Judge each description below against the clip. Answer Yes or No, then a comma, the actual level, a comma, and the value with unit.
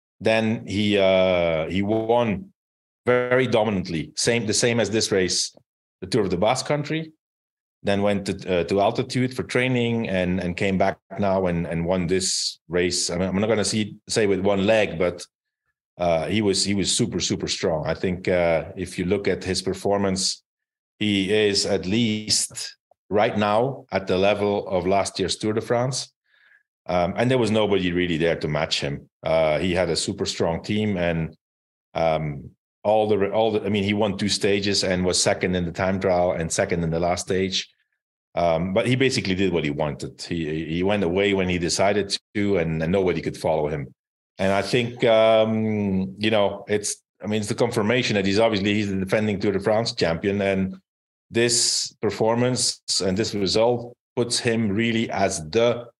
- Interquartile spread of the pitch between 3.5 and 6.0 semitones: No, average, 3.1 semitones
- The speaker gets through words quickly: No, average, 190 wpm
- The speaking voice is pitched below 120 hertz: Yes, low, 100 Hz